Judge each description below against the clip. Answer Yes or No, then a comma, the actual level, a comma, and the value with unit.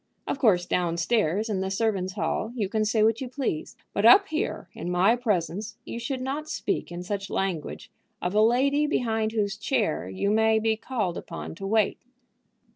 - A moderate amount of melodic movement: Yes, average, 3.8 semitones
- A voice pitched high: Yes, high, 215 Hz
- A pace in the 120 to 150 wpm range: No, average, 190 wpm